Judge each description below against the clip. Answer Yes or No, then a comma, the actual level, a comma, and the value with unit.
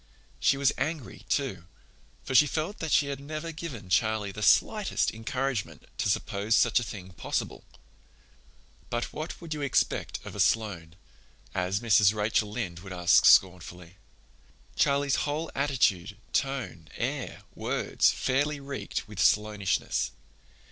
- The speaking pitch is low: Yes, low, 115 Hz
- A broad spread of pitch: Yes, wide, 6.4 semitones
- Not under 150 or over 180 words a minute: No, slow, 135 wpm